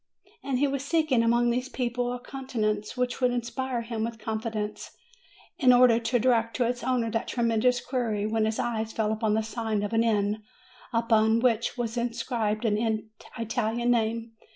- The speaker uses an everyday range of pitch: No, narrow, 1.9 semitones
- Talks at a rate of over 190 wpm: No, average, 175 wpm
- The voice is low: No, high, 230 Hz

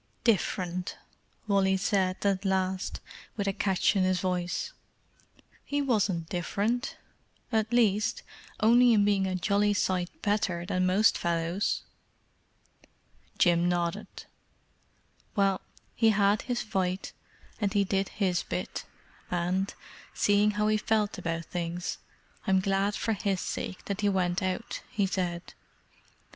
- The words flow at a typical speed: No, slow, 125 wpm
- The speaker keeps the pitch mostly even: Yes, narrow, 2.2 semitones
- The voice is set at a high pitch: Yes, high, 195 Hz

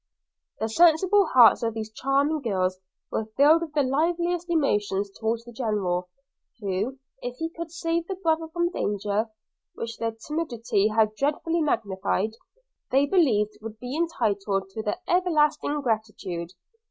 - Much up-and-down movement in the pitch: Yes, wide, 7.3 semitones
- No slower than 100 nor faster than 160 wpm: Yes, average, 140 wpm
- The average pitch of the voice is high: Yes, high, 245 Hz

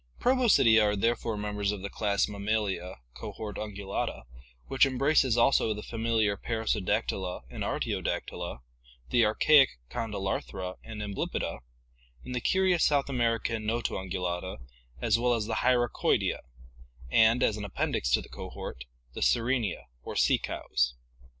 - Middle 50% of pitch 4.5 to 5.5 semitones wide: No, average, 3.2 semitones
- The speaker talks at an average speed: No, slow, 130 wpm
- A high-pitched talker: No, low, 110 Hz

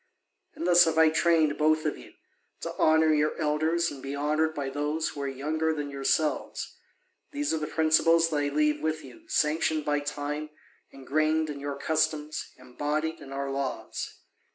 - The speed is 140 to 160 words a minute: No, average, 175 wpm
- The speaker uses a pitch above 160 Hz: No, medium, 155 Hz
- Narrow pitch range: Yes, narrow, 1.6 semitones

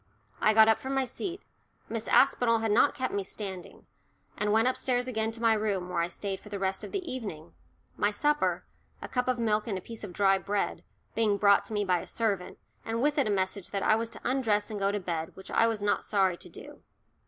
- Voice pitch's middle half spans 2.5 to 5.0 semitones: Yes, average, 2.9 semitones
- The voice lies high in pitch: Yes, high, 215 Hz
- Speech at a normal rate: No, fast, 235 wpm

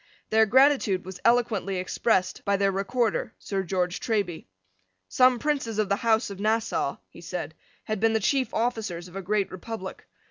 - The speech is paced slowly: No, average, 170 wpm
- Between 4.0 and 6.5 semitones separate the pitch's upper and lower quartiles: No, average, 3.2 semitones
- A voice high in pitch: Yes, high, 215 Hz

